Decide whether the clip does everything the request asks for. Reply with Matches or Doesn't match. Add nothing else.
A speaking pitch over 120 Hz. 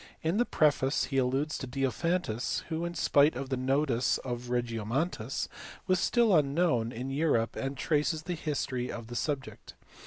Matches